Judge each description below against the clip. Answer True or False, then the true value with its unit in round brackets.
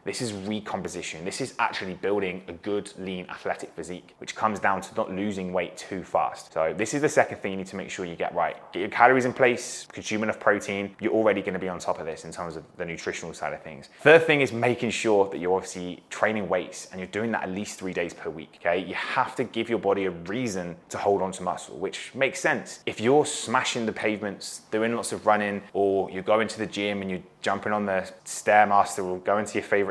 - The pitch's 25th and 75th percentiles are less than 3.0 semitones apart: True (2.4 semitones)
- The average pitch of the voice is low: True (100 Hz)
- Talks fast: True (245 wpm)